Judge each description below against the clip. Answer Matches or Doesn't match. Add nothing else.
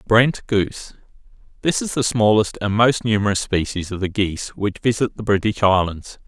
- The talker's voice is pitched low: Matches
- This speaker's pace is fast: Doesn't match